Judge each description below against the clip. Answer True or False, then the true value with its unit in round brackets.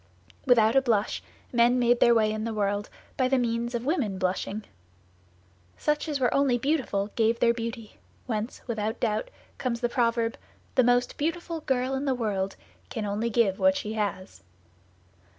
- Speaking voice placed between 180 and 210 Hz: False (235 Hz)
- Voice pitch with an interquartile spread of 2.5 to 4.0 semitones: True (2.9 semitones)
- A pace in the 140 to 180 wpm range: True (170 wpm)